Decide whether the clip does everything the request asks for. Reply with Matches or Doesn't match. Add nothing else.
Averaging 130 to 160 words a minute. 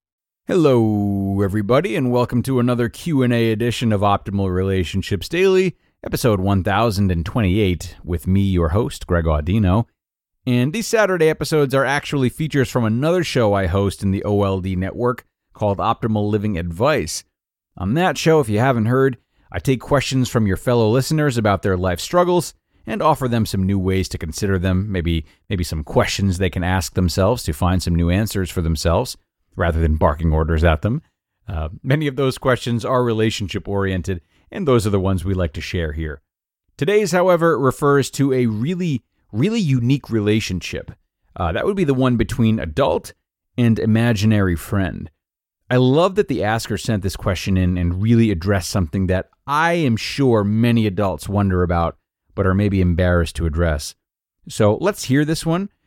Doesn't match